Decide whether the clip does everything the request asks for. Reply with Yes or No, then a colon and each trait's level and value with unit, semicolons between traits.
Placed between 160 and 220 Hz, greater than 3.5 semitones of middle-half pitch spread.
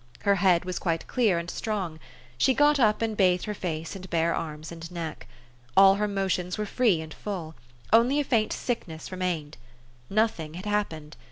Yes: medium, 185 Hz; average, 4.2 semitones